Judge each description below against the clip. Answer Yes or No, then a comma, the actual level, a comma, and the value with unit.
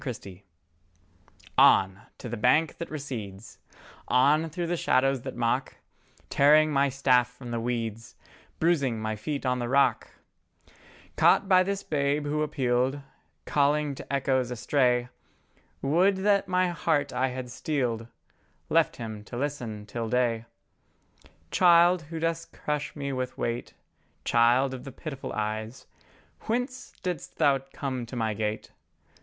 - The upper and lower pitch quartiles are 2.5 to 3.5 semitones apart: No, average, 4.2 semitones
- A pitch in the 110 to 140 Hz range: Yes, low, 135 Hz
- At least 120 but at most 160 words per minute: Yes, average, 140 wpm